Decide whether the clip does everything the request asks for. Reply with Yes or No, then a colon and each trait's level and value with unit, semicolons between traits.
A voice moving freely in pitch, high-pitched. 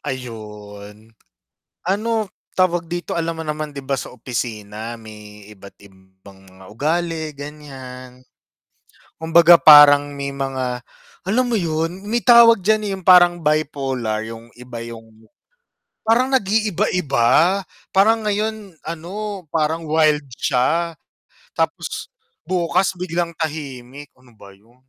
No: wide, 7.0 semitones; medium, 150 Hz